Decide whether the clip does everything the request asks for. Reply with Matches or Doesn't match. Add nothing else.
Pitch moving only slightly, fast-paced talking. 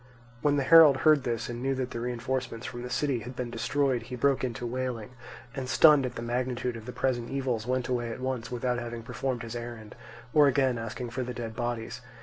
Matches